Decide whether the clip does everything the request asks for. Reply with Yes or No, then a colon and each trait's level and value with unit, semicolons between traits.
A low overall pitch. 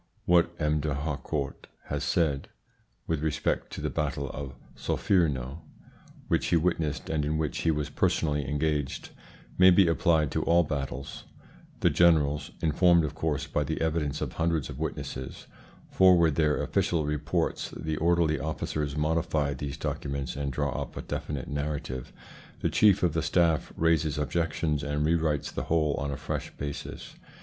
Yes: very low, 75 Hz